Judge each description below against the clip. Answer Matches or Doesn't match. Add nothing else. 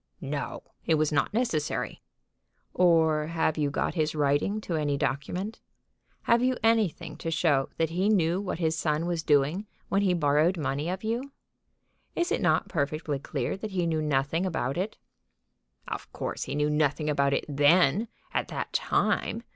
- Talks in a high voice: Doesn't match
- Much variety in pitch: Doesn't match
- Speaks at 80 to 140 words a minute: Doesn't match